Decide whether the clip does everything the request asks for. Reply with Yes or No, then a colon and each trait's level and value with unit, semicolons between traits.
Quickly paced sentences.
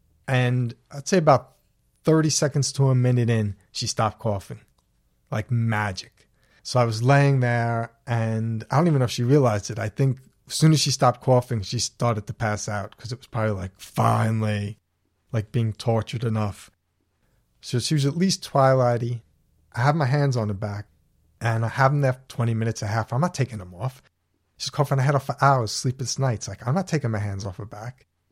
Yes: fast, 210 wpm